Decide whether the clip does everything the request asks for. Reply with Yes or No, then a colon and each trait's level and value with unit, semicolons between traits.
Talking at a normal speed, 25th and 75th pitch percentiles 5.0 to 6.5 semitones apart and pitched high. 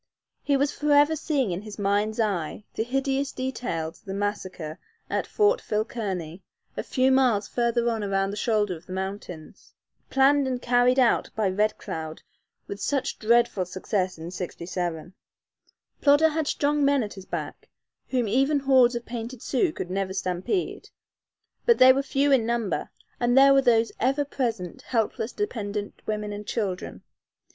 Yes: average, 160 wpm; wide, 5.5 semitones; high, 230 Hz